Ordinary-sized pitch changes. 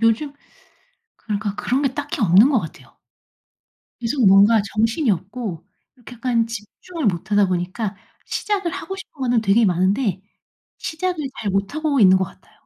No: wide, 5.7 semitones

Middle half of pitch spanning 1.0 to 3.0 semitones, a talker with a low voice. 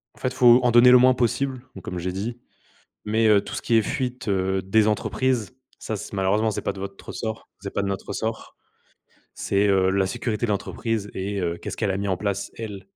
No: average, 3.5 semitones; low, 105 Hz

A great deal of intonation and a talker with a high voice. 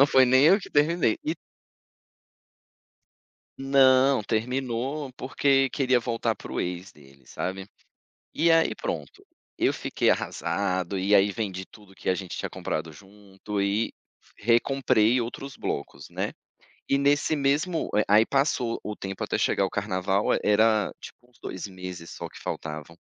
No: wide, 5.9 semitones; low, 110 Hz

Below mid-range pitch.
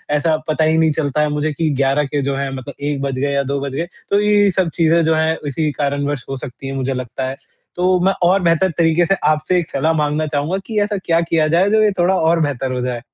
No: medium, 155 Hz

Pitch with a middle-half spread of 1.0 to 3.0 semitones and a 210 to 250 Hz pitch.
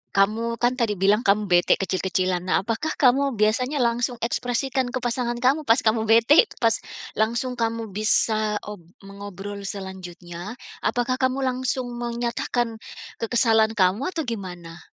No: average, 3.6 semitones; high, 225 Hz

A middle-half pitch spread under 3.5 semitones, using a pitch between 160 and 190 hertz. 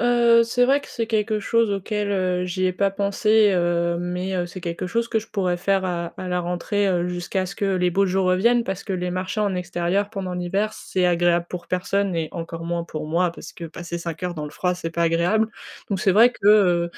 Yes: average, 2.8 semitones; medium, 185 Hz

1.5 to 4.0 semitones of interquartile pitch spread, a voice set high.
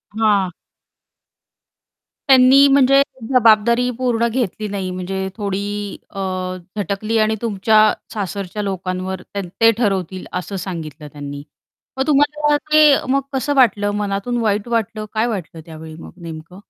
No: average, 4.5 semitones; high, 210 Hz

